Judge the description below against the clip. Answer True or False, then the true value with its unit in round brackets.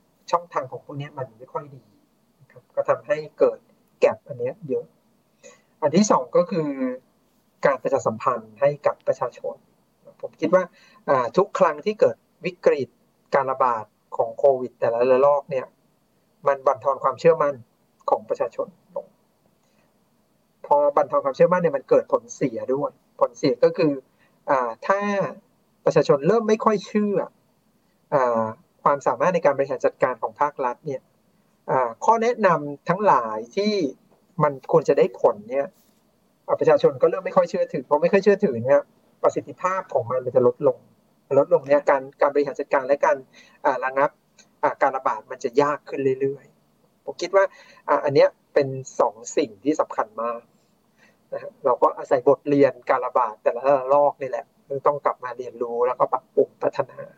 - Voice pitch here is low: False (215 Hz)